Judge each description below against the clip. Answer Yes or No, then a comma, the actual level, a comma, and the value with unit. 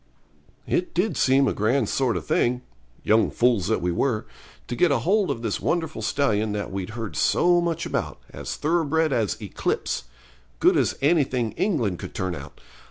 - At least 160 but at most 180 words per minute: Yes, average, 170 wpm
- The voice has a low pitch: Yes, low, 125 Hz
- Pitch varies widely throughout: Yes, wide, 7.0 semitones